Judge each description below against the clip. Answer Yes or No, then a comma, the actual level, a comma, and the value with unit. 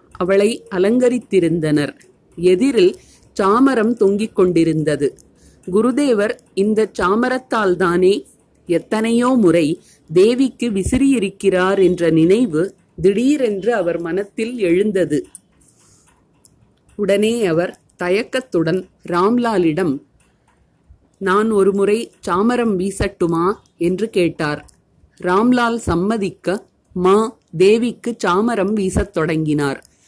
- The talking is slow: Yes, slow, 70 wpm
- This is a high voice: Yes, high, 195 Hz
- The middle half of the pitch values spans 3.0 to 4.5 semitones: Yes, average, 4.1 semitones